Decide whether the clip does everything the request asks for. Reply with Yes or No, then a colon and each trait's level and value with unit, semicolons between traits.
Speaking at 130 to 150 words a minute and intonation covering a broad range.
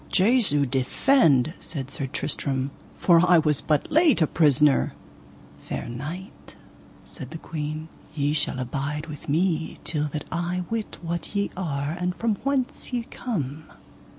No: average, 145 wpm; average, 4.2 semitones